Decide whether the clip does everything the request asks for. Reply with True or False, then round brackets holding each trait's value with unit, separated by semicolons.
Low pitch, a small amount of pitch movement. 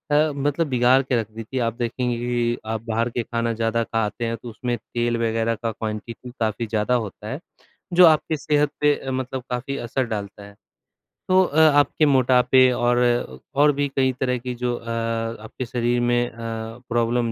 True (120 Hz; 2.3 semitones)